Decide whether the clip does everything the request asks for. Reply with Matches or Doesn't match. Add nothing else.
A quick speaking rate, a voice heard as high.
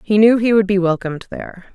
Matches